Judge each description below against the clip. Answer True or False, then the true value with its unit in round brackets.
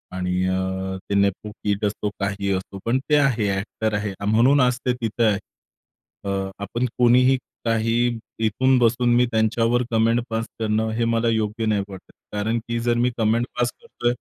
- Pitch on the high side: False (110 Hz)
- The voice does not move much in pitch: False (3.0 semitones)